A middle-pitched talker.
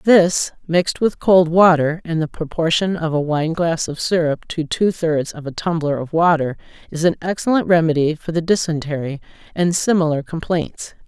Yes: medium, 165 Hz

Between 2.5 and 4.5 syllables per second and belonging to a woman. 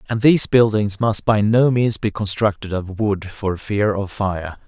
No: 4.3 syllables/s; male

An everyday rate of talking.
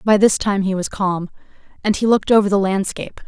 No: fast, 220 wpm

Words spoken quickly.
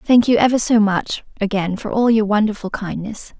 No: average, 195 wpm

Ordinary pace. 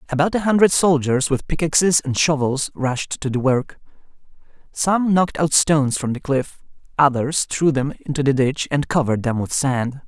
Yes: average, 180 wpm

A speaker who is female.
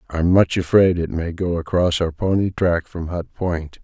No: male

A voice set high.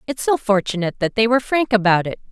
Yes: high, 220 Hz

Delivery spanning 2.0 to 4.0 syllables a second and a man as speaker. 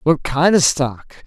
Yes: 3.4 syllables/s; male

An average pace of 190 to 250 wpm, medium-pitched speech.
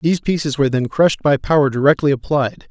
Yes: average, 200 wpm; medium, 145 Hz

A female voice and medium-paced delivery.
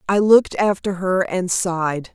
Yes: female; average, 170 wpm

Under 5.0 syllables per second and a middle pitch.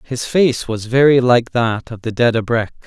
No: 4.5 syllables/s; low, 120 Hz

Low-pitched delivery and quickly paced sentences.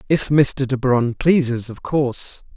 No: low, 130 Hz; average, 165 wpm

